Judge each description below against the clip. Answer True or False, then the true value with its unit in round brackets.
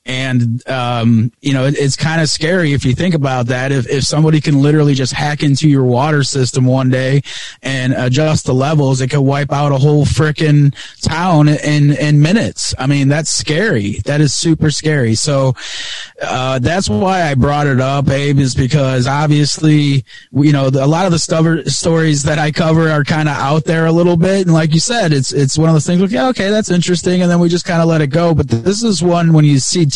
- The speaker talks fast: True (230 wpm)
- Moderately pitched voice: True (145 Hz)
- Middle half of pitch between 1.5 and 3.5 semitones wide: True (3.2 semitones)